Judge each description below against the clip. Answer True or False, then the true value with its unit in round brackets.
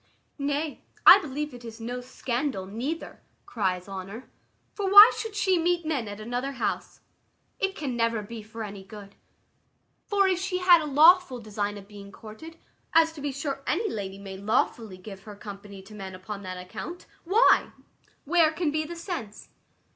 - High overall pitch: True (245 Hz)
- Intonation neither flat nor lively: False (8.0 semitones)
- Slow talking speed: False (175 wpm)